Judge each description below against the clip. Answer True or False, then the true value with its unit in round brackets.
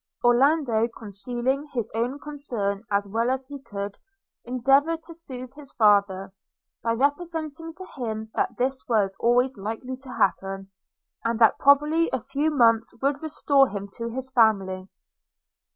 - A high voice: True (245 Hz)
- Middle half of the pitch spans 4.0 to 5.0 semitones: True (4.4 semitones)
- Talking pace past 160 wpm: False (145 wpm)